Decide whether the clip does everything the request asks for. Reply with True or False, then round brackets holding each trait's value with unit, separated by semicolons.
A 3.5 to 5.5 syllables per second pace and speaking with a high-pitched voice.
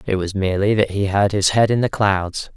False (5.4 syllables/s; 100 Hz)